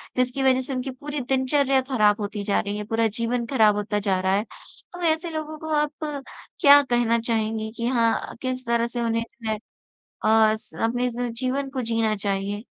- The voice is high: Yes, high, 235 Hz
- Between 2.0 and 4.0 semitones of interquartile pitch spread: Yes, average, 3.5 semitones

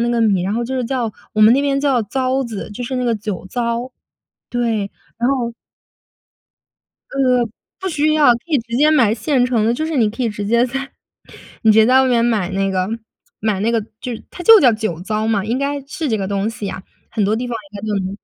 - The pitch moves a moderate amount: Yes, average, 3.6 semitones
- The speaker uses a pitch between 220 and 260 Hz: Yes, high, 235 Hz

